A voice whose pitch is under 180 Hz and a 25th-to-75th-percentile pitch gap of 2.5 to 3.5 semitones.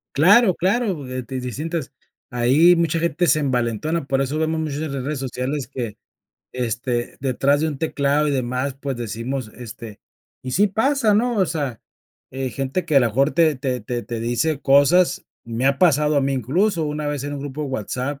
No: medium, 140 Hz; average, 3.9 semitones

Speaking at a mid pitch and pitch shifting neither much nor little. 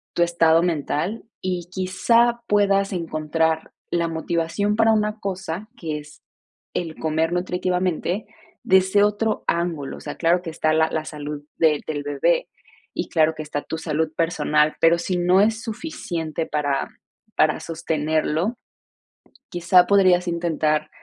Yes: medium, 170 Hz; average, 3.2 semitones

